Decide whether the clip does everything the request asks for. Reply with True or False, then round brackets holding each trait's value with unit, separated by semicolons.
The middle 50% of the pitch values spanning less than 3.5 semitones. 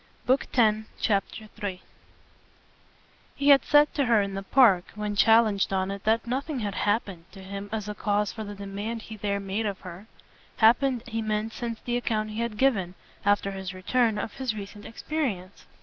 True (2.8 semitones)